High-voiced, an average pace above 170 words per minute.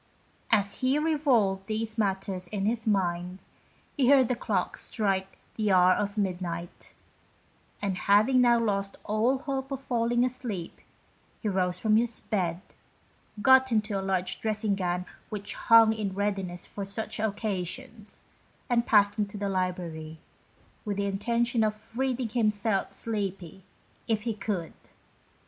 No: high, 210 Hz; average, 140 wpm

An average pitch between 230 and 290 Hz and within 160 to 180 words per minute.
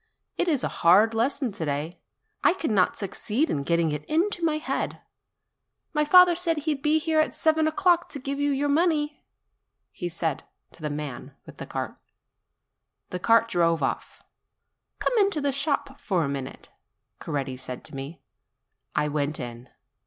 Yes: high, 235 Hz; average, 170 wpm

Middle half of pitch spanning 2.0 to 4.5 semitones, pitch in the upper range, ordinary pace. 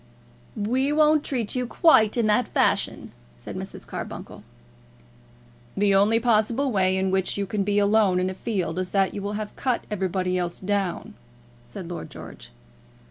Yes: average, 3.3 semitones; high, 205 Hz; average, 165 wpm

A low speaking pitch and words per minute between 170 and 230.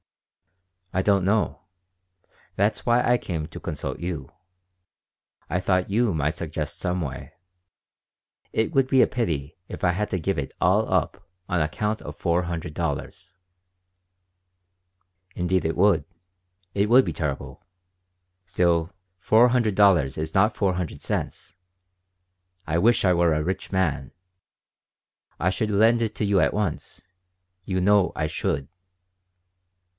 No: very low, 90 Hz; average, 140 wpm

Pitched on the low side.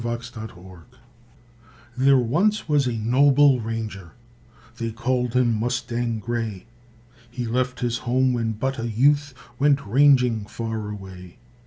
Yes: low, 120 Hz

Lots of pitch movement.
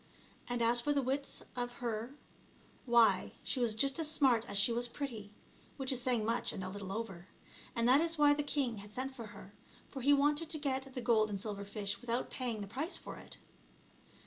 No: average, 4.2 semitones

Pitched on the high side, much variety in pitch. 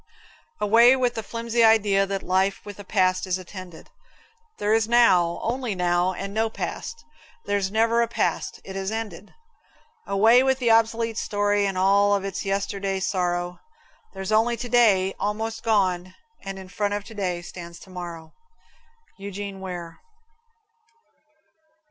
No: high, 200 Hz; average, 3.2 semitones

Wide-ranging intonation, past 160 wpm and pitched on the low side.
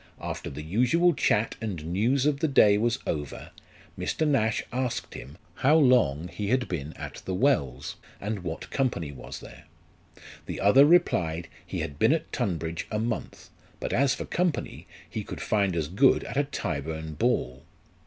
Yes: wide, 8.7 semitones; average, 170 wpm; low, 105 Hz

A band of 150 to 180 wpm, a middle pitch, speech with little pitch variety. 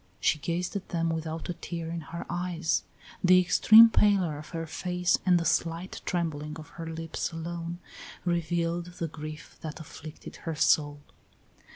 Yes: average, 160 wpm; medium, 165 Hz; narrow, 1.6 semitones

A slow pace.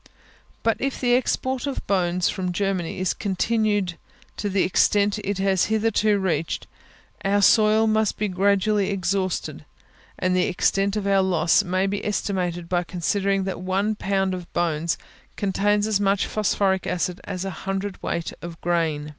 No: average, 155 wpm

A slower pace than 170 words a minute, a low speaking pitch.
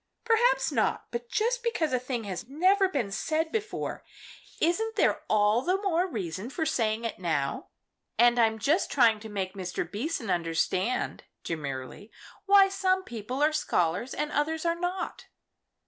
No: average, 155 wpm; very high, 255 Hz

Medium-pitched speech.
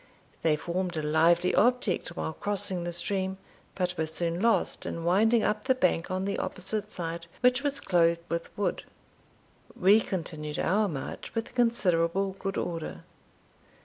Yes: medium, 180 Hz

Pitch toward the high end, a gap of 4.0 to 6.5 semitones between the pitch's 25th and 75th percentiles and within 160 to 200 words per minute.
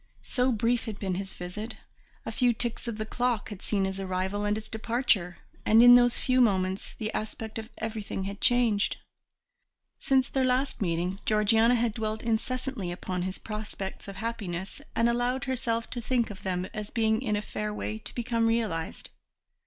No: high, 220 Hz; average, 3.3 semitones; average, 180 wpm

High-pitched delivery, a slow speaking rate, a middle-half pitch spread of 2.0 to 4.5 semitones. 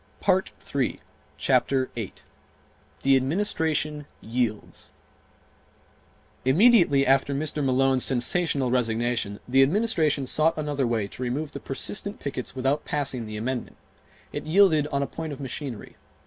No: low, 135 Hz; slow, 120 wpm; average, 3.3 semitones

